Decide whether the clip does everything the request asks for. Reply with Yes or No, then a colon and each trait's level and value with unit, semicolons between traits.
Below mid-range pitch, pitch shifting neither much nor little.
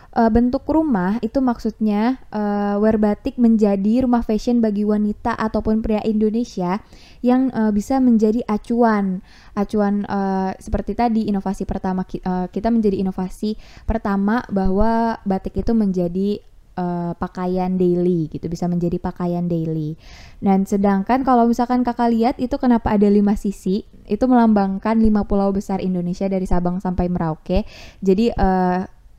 No: high, 205 Hz; average, 3.2 semitones